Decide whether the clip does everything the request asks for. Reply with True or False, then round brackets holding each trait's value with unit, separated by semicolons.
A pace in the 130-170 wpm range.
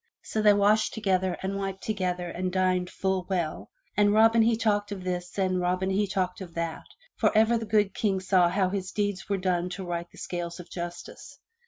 False (205 wpm)